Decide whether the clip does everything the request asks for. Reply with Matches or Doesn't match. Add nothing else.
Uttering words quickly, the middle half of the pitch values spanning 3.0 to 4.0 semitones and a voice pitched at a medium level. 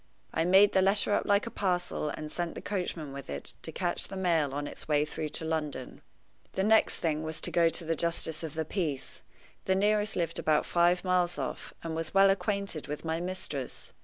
Matches